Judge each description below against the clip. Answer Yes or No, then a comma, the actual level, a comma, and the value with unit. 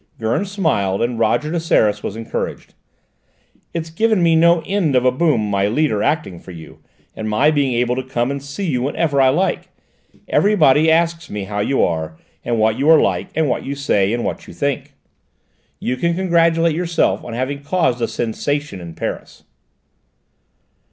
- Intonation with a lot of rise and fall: Yes, wide, 6.4 semitones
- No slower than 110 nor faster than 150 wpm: No, average, 180 wpm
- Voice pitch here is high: No, medium, 140 Hz